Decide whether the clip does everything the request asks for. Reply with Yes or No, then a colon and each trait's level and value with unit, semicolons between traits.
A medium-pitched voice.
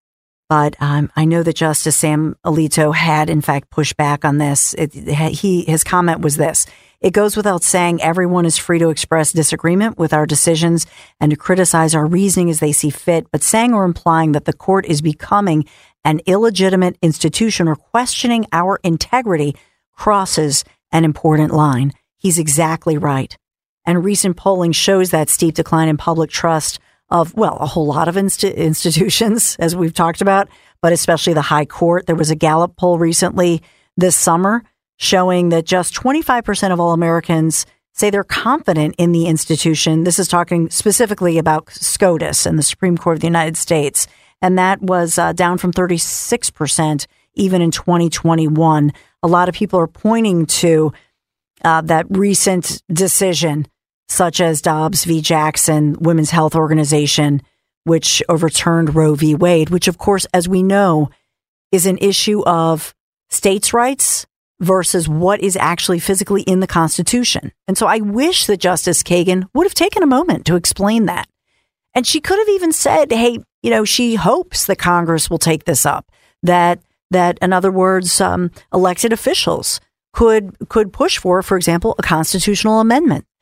Yes: medium, 170 Hz